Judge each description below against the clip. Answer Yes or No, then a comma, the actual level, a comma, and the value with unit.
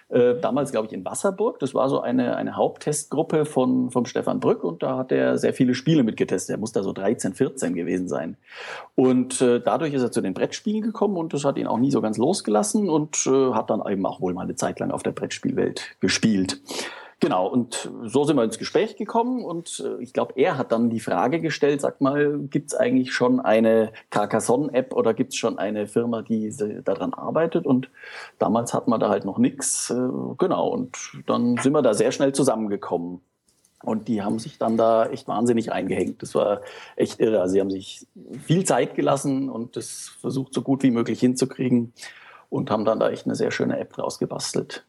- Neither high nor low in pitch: No, low, 125 Hz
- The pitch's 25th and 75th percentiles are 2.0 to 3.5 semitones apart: No, average, 4.2 semitones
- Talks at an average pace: No, fast, 205 wpm